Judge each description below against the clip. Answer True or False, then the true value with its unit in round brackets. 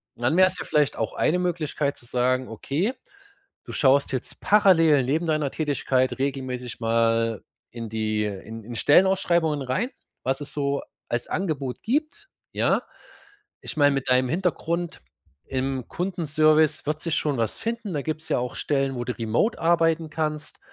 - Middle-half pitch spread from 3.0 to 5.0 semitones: True (4.6 semitones)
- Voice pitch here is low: False (145 Hz)